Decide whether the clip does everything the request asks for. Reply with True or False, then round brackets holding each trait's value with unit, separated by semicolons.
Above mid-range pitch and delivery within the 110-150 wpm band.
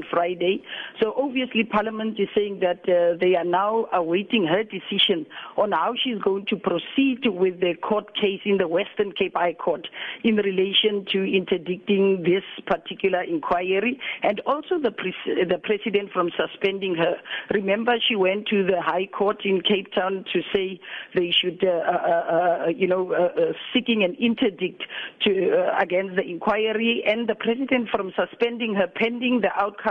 False (200 Hz; 170 wpm)